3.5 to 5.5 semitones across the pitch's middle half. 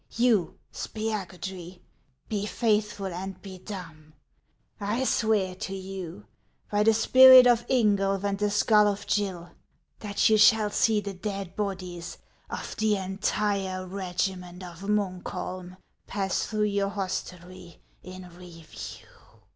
No: narrow, 2.4 semitones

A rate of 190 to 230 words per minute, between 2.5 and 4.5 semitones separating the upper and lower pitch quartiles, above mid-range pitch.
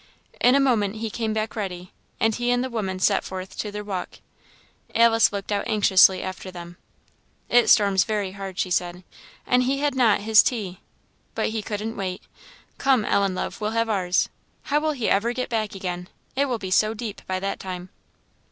Yes: average, 200 wpm; average, 3.5 semitones; high, 210 Hz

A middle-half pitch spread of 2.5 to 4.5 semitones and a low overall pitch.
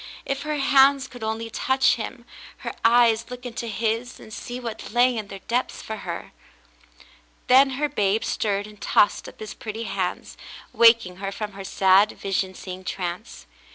No: average, 3.8 semitones; high, 225 Hz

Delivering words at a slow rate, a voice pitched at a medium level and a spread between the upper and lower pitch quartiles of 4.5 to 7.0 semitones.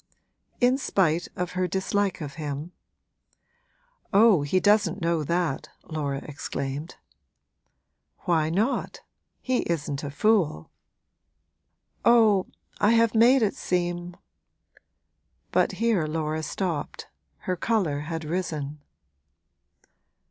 Yes: slow, 105 wpm; medium, 175 Hz; average, 5.1 semitones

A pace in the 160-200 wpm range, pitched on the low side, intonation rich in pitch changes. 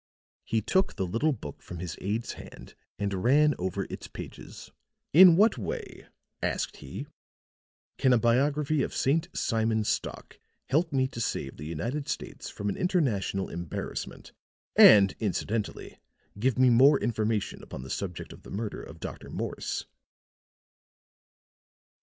No: average, 140 wpm; low, 115 Hz; wide, 6.2 semitones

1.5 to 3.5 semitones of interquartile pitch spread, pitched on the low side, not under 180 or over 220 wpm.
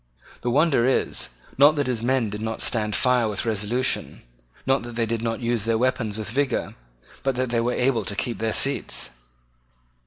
Yes: narrow, 2.6 semitones; low, 120 Hz; average, 190 wpm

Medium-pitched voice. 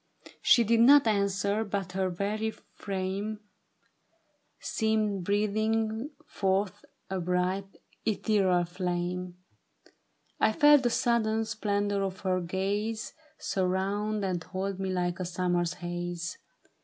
No: high, 195 Hz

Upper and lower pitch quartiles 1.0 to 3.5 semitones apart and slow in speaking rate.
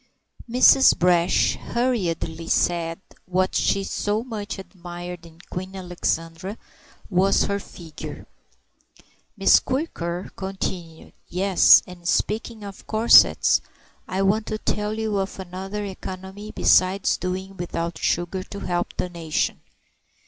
Yes: average, 2.7 semitones; slow, 115 wpm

